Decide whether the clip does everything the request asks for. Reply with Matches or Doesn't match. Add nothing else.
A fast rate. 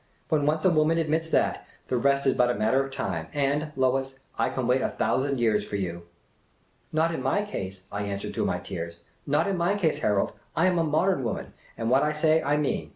Matches